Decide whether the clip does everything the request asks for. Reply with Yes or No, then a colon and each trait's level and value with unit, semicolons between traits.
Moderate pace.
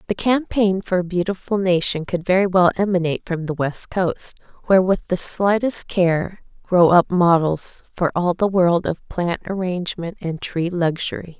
Yes: average, 170 wpm